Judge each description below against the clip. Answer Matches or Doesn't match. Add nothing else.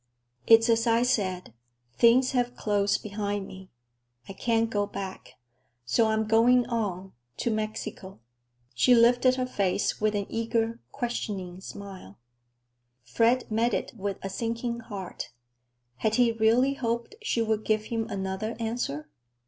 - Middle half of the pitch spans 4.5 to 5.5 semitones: Doesn't match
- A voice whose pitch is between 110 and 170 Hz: Doesn't match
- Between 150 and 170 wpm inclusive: Doesn't match